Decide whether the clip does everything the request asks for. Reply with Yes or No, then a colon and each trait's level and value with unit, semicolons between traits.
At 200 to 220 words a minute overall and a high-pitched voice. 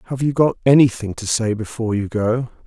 No: fast, 205 wpm; low, 120 Hz